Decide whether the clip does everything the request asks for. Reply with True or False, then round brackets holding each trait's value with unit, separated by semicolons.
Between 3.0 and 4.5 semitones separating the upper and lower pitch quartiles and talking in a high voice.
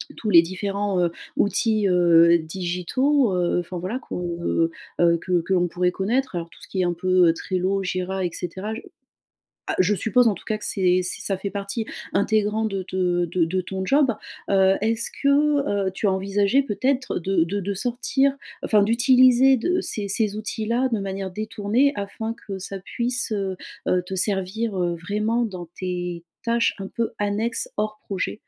True (3.5 semitones; 195 Hz)